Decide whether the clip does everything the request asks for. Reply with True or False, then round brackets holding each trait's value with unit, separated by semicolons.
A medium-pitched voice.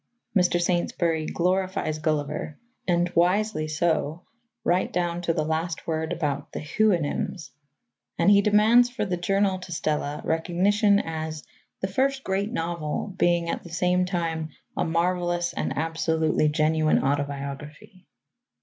True (170 Hz)